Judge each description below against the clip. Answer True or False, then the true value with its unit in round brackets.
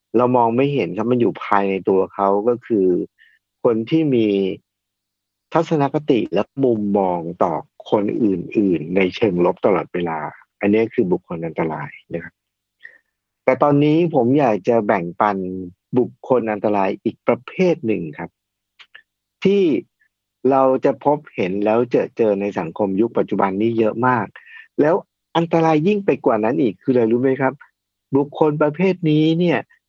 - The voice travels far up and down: True (7.6 semitones)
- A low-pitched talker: True (125 Hz)